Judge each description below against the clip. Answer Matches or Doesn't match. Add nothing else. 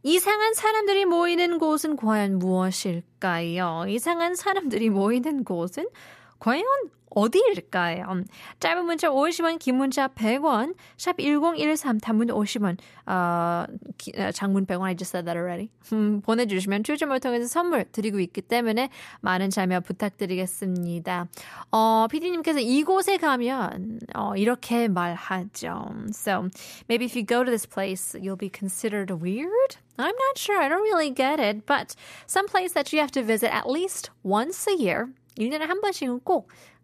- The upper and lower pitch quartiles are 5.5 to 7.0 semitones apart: Doesn't match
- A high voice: Matches